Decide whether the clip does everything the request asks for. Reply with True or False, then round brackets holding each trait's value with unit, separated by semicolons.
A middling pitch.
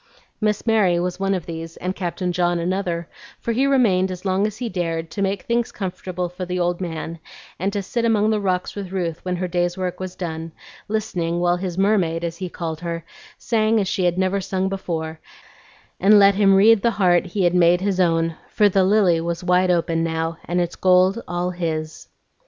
True (180 Hz)